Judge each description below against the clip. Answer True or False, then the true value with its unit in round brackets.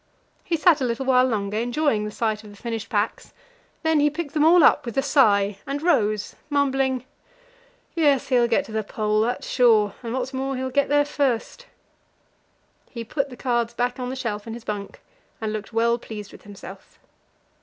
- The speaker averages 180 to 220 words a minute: True (195 wpm)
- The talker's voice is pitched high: True (245 Hz)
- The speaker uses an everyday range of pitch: True (4.2 semitones)